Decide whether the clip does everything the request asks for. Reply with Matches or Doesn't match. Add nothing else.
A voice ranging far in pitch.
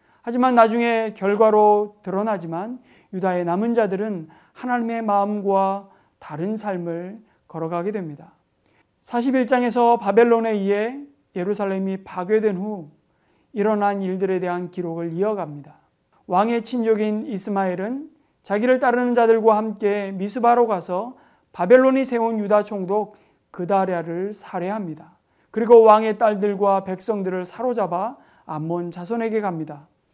Doesn't match